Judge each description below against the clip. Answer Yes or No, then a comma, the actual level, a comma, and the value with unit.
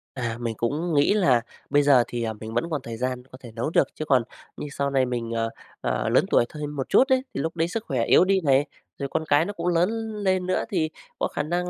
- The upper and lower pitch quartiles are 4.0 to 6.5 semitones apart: Yes, wide, 5.5 semitones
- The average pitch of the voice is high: No, medium, 145 Hz